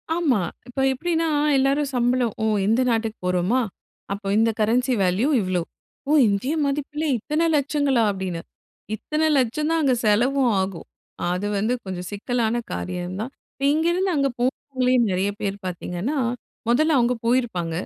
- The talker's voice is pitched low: No, high, 245 Hz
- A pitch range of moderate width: No, wide, 5.8 semitones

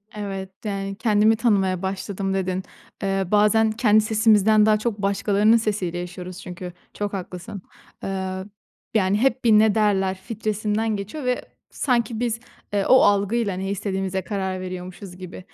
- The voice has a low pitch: No, high, 200 Hz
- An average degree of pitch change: No, narrow, 2.3 semitones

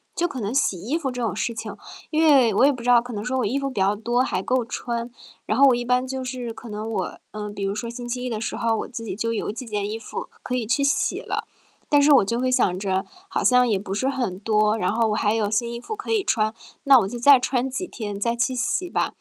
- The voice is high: Yes, high, 235 Hz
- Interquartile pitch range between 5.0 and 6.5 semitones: No, average, 3.3 semitones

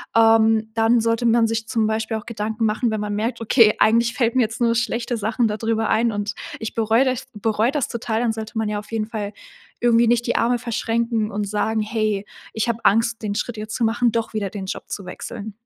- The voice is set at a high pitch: Yes, high, 225 Hz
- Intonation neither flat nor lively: No, narrow, 1.4 semitones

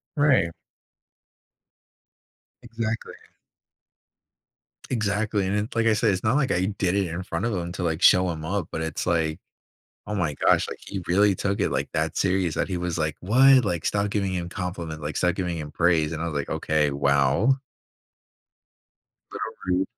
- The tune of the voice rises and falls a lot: No, average, 4.1 semitones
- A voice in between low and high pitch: No, very low, 90 Hz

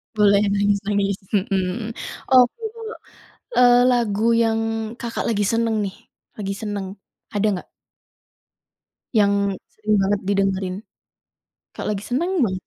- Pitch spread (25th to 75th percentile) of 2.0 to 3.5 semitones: Yes, narrow, 2.6 semitones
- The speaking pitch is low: No, high, 205 Hz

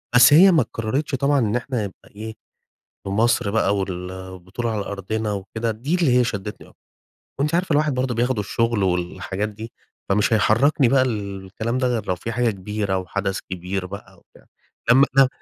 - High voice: No, low, 110 Hz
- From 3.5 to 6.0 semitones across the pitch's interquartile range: Yes, average, 4.2 semitones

